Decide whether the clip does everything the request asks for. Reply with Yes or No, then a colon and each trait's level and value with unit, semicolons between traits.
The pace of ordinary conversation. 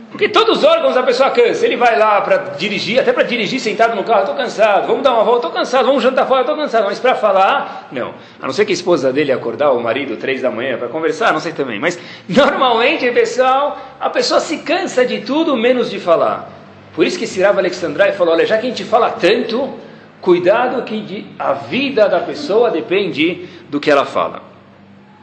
No: fast, 210 wpm